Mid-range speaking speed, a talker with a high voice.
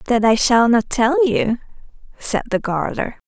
Yes: average, 165 wpm; high, 240 Hz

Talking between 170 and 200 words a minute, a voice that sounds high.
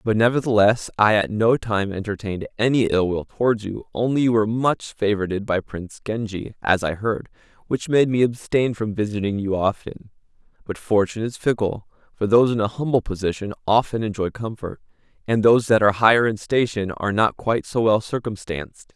No: average, 180 wpm; low, 110 Hz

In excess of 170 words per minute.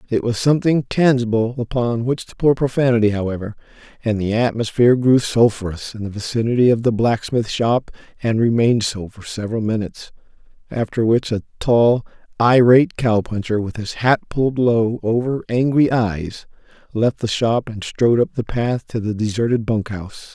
No: average, 165 wpm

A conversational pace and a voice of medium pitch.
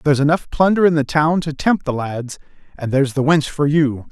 No: fast, 235 wpm; medium, 145 Hz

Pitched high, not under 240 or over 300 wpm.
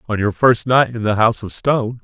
No: low, 115 Hz; fast, 265 wpm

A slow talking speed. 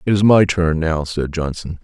No: fast, 230 wpm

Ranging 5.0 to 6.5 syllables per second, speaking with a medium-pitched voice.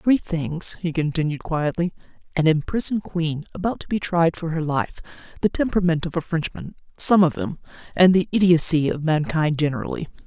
Yes: 5.5 syllables/s; medium, 165 Hz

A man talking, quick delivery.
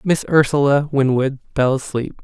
No: male; slow, 135 wpm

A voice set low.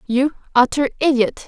No: very high, 265 Hz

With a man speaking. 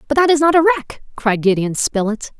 No: female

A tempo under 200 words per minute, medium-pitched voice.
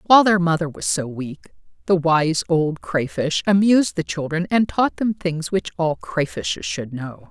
Yes: average, 180 wpm; medium, 150 Hz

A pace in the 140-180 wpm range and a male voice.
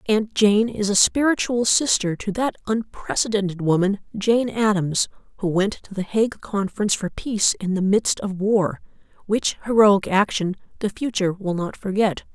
No: average, 160 wpm; female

